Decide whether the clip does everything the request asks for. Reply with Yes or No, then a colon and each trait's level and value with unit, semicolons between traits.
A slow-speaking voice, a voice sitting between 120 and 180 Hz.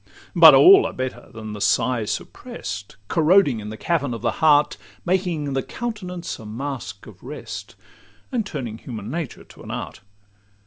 No: average, 165 wpm; low, 135 Hz